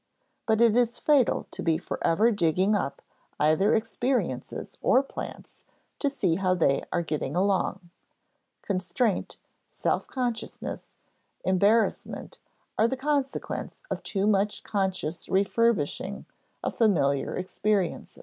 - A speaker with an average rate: No, slow, 115 wpm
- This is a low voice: No, high, 200 Hz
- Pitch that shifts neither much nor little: Yes, average, 4.4 semitones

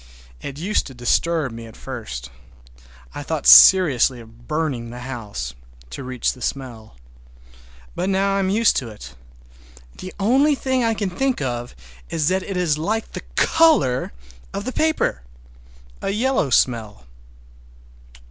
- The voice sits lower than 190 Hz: Yes, medium, 140 Hz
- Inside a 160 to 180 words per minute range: No, average, 145 wpm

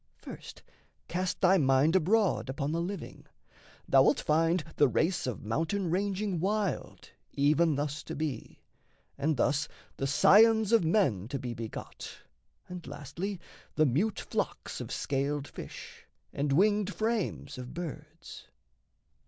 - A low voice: No, medium, 160 Hz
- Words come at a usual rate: No, slow, 130 wpm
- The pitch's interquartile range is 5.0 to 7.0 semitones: Yes, wide, 5.6 semitones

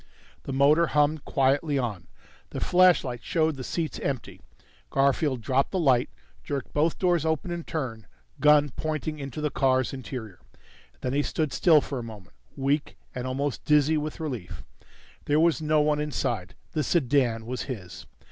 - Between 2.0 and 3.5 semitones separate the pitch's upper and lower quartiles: Yes, average, 3.1 semitones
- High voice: No, medium, 140 Hz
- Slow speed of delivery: No, average, 160 wpm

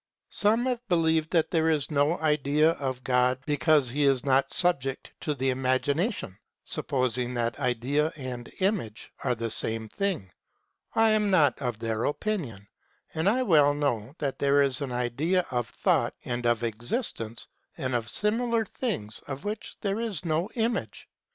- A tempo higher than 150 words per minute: Yes, average, 160 wpm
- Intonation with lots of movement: Yes, wide, 6.1 semitones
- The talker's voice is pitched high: No, medium, 140 Hz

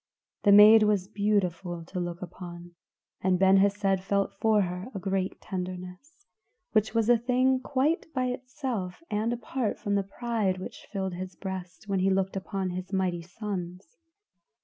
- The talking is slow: No, average, 160 wpm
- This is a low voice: No, high, 195 Hz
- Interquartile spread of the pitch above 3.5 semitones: No, average, 3.1 semitones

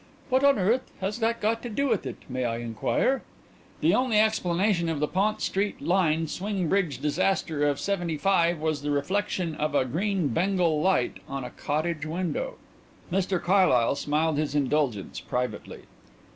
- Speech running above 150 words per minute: Yes, average, 160 wpm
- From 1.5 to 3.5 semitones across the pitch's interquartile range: No, average, 5.2 semitones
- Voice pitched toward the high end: No, medium, 170 Hz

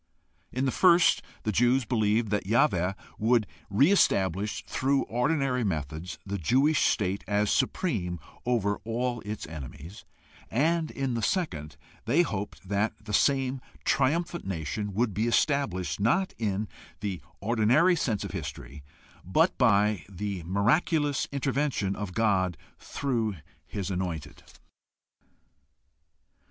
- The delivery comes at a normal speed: No, slow, 120 wpm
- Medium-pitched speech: No, low, 110 Hz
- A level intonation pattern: No, wide, 5.6 semitones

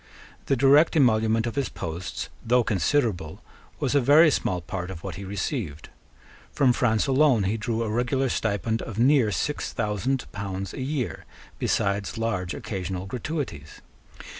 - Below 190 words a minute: Yes, average, 150 wpm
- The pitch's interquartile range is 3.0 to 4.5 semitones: No, wide, 5.5 semitones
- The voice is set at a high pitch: No, low, 110 Hz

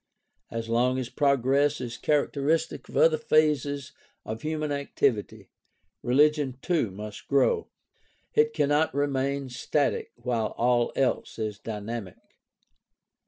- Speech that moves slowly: Yes, slow, 115 wpm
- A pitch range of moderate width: Yes, average, 3.8 semitones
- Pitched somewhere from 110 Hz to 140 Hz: Yes, low, 135 Hz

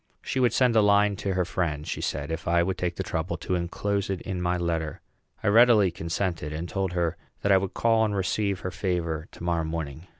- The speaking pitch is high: No, very low, 90 Hz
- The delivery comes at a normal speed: No, fast, 230 wpm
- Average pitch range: Yes, average, 3.2 semitones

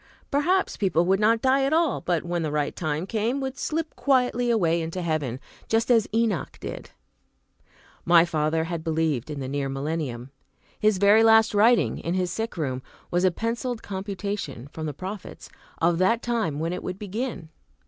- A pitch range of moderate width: No, wide, 6.0 semitones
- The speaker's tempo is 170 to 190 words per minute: Yes, average, 180 wpm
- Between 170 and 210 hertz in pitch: Yes, medium, 185 Hz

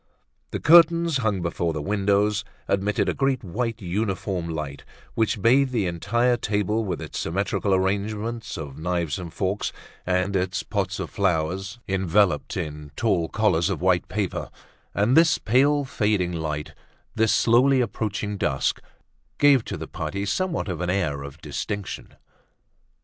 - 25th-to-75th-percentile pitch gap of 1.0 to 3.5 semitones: No, average, 4.3 semitones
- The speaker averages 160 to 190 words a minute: No, average, 145 wpm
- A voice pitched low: Yes, low, 100 Hz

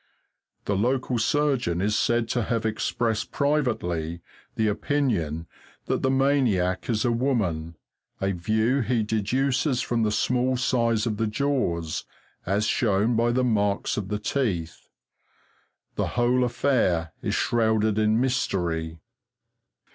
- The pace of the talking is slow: Yes, slow, 130 wpm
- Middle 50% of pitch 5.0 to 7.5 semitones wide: No, average, 4.3 semitones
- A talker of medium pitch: No, low, 110 Hz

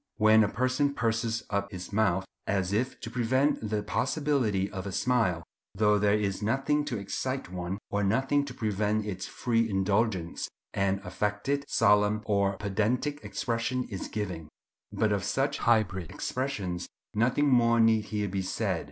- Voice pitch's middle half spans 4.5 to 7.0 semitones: No, average, 3.8 semitones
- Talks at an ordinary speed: Yes, average, 155 wpm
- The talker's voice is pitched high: No, low, 105 Hz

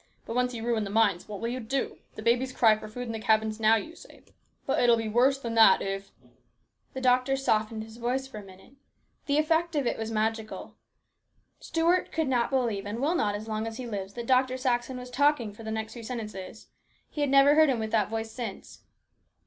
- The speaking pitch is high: Yes, high, 230 Hz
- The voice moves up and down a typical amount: Yes, average, 3.1 semitones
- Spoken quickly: Yes, fast, 230 wpm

